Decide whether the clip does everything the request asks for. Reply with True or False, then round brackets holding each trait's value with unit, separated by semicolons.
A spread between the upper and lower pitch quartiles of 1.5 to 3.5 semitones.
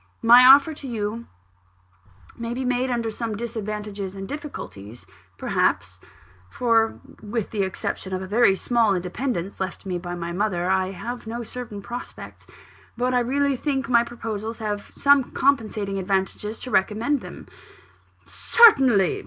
False (4.2 semitones)